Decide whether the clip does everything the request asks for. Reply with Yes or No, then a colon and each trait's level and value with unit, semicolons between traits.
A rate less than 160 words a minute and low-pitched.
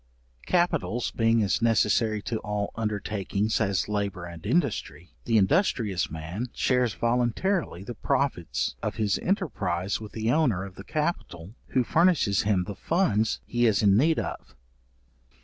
Yes: average, 145 wpm; low, 110 Hz